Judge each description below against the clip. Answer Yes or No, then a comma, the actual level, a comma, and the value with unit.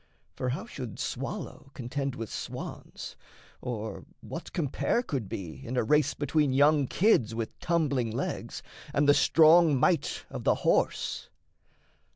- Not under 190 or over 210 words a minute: No, average, 140 wpm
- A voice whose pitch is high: No, medium, 140 Hz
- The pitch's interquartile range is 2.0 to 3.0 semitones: No, average, 4.2 semitones